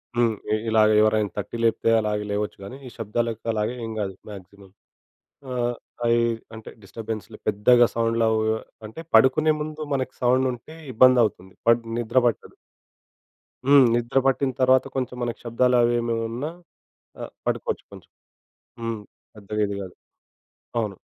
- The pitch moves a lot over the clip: No, average, 2.8 semitones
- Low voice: Yes, low, 115 Hz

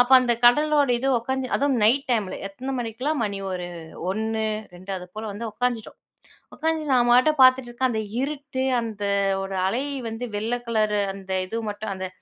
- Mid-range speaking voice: No, high, 235 Hz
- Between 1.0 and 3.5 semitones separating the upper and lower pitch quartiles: No, average, 3.9 semitones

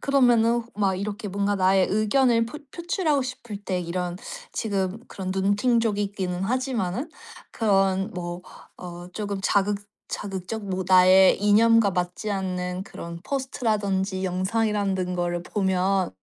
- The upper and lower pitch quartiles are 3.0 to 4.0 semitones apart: Yes, average, 3.3 semitones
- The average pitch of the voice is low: No, high, 195 Hz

